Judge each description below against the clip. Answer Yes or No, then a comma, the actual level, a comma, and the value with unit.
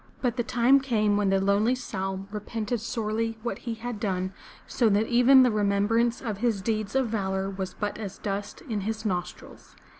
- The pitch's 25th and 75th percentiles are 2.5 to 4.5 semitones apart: Yes, average, 2.9 semitones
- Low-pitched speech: No, high, 215 Hz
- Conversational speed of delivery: Yes, average, 185 wpm